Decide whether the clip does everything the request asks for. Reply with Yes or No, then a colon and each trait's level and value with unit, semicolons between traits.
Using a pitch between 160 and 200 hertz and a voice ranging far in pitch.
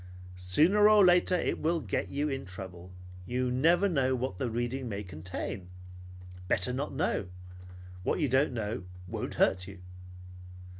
No: low, 125 Hz; wide, 8.1 semitones